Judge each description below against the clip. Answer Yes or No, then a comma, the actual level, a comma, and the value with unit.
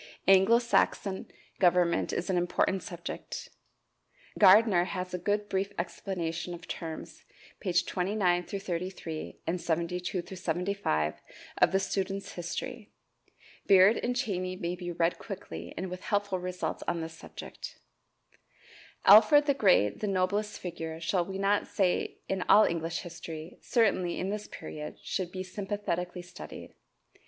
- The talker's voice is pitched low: No, medium, 185 Hz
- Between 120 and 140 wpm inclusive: Yes, slow, 135 wpm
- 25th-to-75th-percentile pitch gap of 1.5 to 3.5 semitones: Yes, narrow, 2.5 semitones